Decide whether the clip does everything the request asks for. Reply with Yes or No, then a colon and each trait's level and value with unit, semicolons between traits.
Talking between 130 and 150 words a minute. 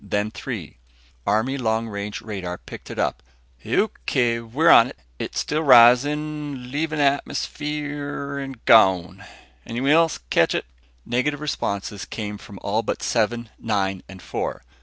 Yes: slow, 135 wpm